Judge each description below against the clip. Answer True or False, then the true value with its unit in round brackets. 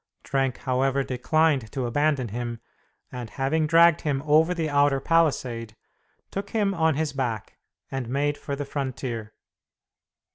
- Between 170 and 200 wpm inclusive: False (140 wpm)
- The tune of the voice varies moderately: True (3.7 semitones)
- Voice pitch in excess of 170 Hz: False (140 Hz)